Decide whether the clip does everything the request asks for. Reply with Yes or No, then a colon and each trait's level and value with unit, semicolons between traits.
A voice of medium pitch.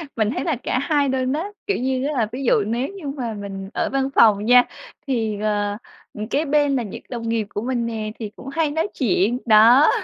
No: high, 245 Hz